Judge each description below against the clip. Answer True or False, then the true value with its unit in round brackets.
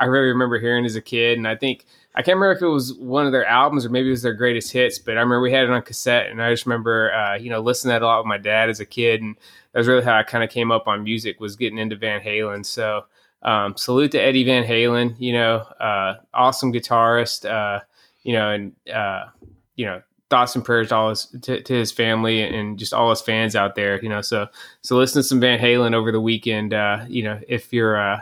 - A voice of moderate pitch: False (115 Hz)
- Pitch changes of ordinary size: False (2.3 semitones)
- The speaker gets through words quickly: True (265 wpm)